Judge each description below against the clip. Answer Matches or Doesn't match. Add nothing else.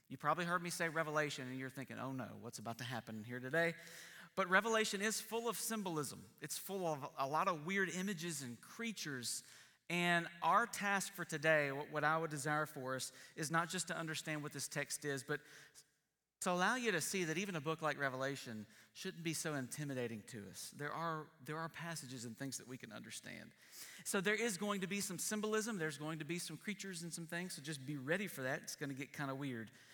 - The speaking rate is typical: Doesn't match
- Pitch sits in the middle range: Matches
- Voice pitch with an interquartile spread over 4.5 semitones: Matches